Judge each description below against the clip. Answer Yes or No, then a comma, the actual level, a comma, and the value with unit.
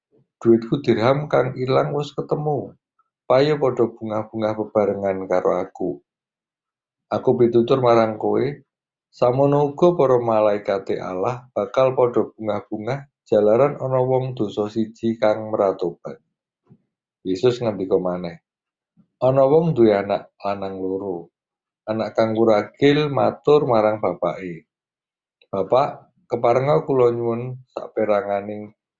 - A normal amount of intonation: Yes, average, 3.8 semitones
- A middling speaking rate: Yes, average, 105 wpm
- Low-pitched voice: Yes, low, 115 Hz